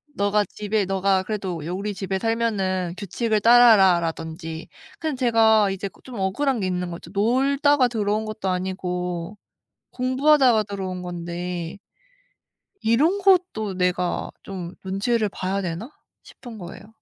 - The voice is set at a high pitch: Yes, high, 200 Hz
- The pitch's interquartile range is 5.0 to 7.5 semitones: No, average, 4.0 semitones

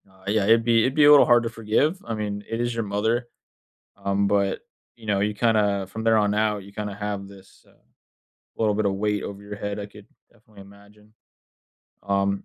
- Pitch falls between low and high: No, low, 105 Hz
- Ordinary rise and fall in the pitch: No, narrow, 2.0 semitones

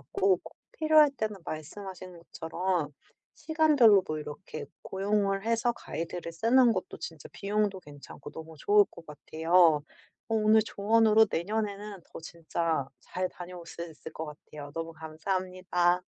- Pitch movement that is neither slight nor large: Yes, average, 4.5 semitones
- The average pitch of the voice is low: No, medium, 185 Hz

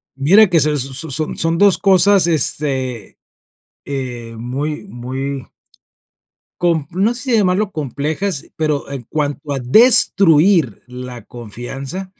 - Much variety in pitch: Yes, wide, 5.8 semitones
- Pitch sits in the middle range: Yes, medium, 150 Hz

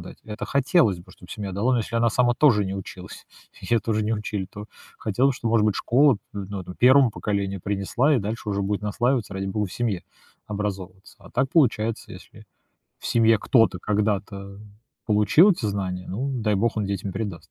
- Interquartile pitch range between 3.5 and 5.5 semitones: No, average, 3.0 semitones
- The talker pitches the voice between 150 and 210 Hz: No, low, 105 Hz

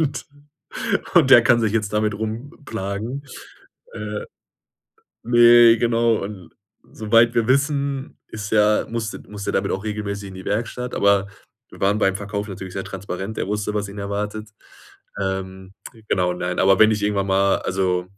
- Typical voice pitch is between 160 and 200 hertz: No, low, 105 Hz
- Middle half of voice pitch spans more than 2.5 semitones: Yes, average, 2.9 semitones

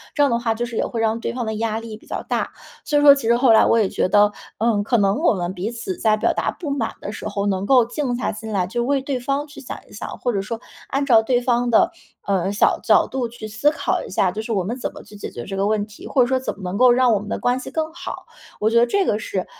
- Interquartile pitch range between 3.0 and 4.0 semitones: Yes, average, 3.4 semitones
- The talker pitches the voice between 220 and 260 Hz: Yes, high, 230 Hz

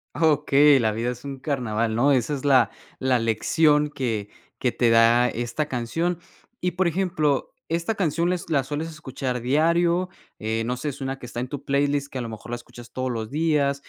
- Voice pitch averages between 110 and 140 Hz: Yes, low, 135 Hz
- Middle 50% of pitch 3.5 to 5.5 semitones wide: Yes, average, 4.1 semitones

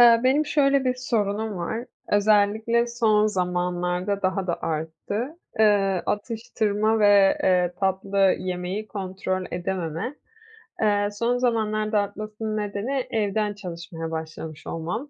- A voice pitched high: Yes, high, 205 Hz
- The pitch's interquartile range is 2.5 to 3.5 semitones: Yes, average, 3.2 semitones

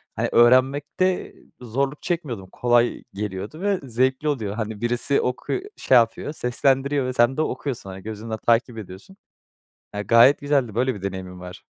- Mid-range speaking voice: No, low, 120 Hz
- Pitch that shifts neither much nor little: Yes, average, 4.4 semitones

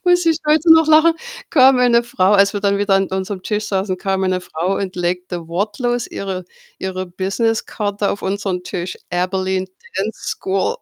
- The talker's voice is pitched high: Yes, high, 195 Hz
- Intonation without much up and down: No, average, 3.7 semitones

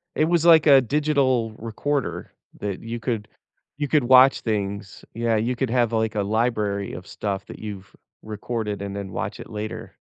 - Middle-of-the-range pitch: No, low, 115 Hz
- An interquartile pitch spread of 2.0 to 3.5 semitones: No, average, 4.0 semitones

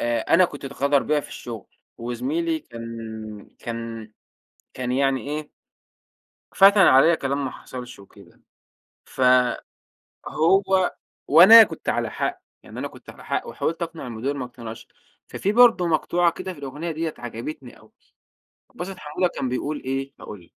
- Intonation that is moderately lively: No, wide, 5.7 semitones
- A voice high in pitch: No, medium, 140 Hz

